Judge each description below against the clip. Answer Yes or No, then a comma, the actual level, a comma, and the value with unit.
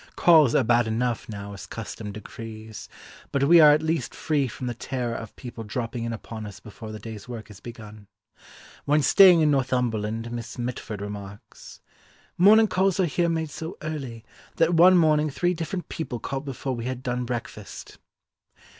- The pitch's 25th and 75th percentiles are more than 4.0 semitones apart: Yes, wide, 5.6 semitones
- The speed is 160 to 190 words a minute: Yes, average, 175 wpm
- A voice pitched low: Yes, low, 125 Hz